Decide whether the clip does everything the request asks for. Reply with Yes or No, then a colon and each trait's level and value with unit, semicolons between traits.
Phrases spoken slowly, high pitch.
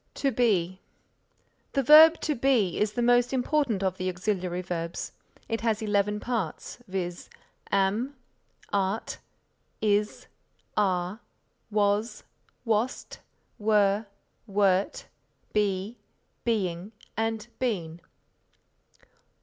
Yes: slow, 95 wpm; high, 210 Hz